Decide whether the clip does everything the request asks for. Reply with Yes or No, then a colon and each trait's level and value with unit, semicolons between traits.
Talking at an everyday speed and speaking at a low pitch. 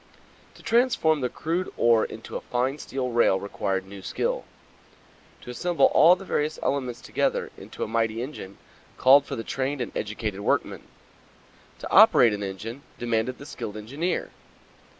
Yes: average, 155 wpm; low, 125 Hz